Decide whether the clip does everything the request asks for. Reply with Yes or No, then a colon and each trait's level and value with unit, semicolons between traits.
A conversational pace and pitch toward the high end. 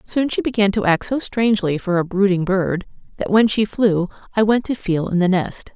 No: fast, 230 wpm; high, 200 Hz